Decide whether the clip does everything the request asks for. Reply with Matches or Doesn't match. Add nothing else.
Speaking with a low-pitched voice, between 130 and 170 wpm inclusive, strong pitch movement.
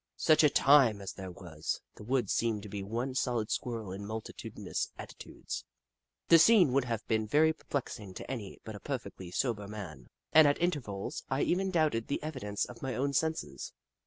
Doesn't match